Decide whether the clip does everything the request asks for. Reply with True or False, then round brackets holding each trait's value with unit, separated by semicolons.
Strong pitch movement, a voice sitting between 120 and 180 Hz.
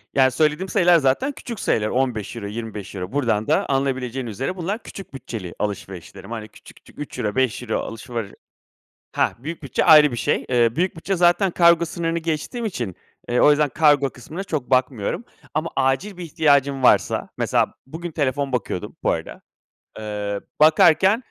True (6.0 semitones; 135 Hz)